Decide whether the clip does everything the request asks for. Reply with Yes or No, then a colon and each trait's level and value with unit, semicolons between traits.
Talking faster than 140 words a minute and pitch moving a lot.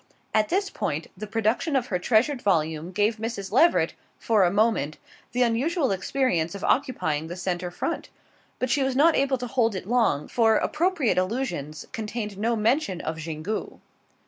Yes: average, 170 wpm; wide, 6.0 semitones